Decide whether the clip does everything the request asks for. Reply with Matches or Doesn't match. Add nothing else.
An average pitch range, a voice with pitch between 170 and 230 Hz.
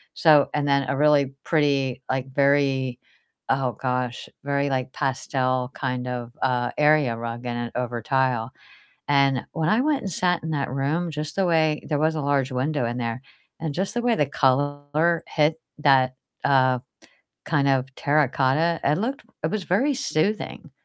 Doesn't match